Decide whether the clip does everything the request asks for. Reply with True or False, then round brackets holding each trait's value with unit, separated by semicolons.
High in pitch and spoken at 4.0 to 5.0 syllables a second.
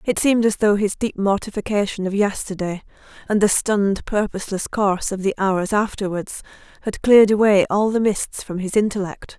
False (200 Hz; 5.4 syllables/s)